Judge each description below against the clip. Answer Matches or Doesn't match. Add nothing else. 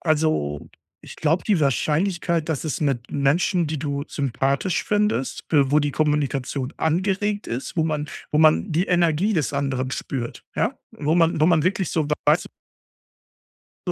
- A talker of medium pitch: Matches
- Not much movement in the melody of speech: Doesn't match